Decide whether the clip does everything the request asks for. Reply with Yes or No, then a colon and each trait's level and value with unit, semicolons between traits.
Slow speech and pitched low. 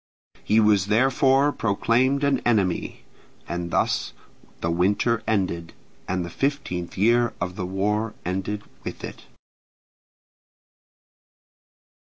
Yes: slow, 105 wpm; low, 105 Hz